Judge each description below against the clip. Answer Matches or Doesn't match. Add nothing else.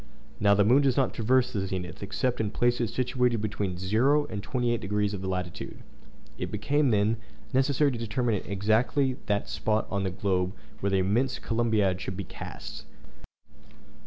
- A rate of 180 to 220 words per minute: Doesn't match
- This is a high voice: Doesn't match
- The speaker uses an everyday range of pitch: Matches